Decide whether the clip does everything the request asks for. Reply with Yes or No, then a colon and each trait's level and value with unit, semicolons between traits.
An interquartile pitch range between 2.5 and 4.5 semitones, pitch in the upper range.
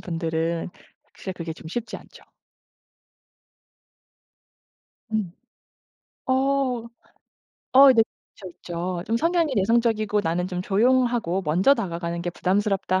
No: wide, 5.6 semitones; high, 195 Hz